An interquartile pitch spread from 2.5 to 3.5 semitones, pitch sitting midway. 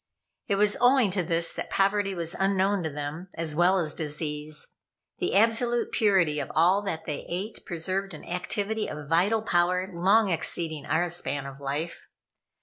No: average, 3.9 semitones; medium, 175 Hz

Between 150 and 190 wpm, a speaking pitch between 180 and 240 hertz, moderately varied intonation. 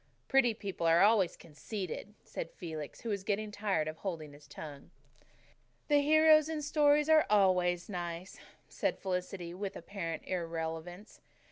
No: average, 140 wpm; high, 190 Hz; average, 4.5 semitones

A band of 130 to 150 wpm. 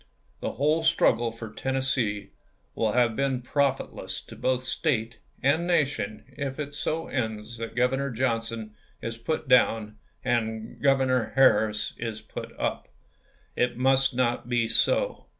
Yes: average, 140 wpm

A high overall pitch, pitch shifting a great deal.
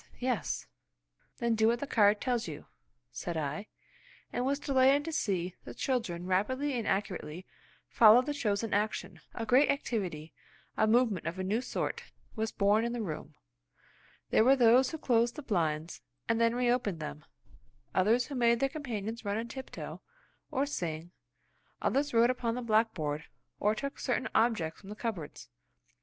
No: high, 225 Hz; average, 4.6 semitones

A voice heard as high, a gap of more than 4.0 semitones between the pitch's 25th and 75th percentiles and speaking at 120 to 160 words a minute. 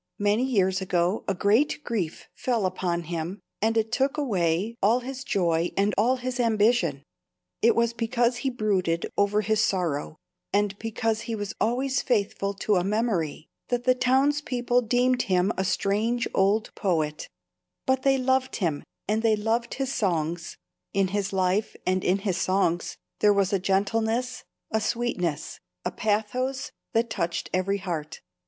Yes: high, 210 Hz; average, 4.5 semitones; average, 155 wpm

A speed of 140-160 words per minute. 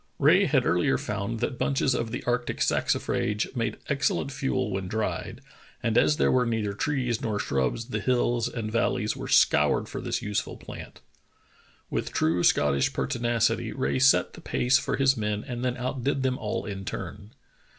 No: average, 175 wpm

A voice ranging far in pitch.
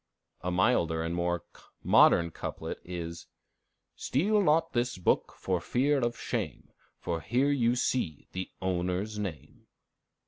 Yes: wide, 6.4 semitones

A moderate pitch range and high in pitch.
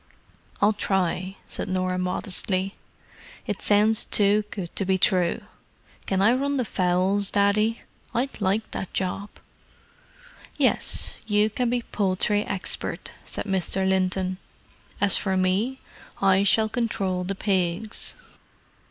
No: narrow, 2.3 semitones; high, 195 Hz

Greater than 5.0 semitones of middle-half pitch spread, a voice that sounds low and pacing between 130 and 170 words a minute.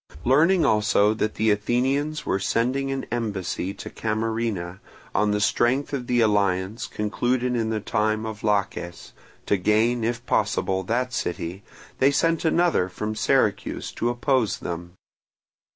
No: average, 3.5 semitones; low, 110 Hz; average, 140 wpm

